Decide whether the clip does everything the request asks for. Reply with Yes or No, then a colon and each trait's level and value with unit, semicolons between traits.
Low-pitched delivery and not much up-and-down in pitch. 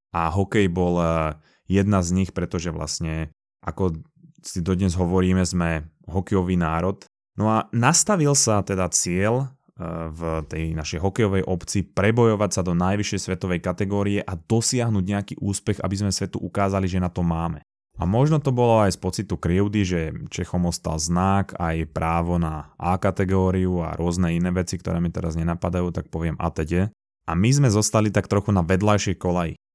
No: very low, 95 Hz; average, 3.0 semitones